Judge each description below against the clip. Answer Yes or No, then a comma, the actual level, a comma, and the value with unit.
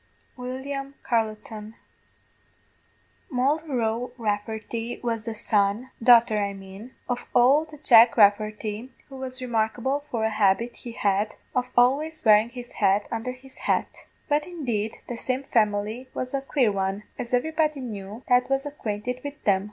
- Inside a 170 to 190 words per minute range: No, average, 145 wpm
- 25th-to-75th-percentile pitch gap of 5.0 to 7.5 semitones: No, average, 3.5 semitones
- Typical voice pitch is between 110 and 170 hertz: No, high, 240 Hz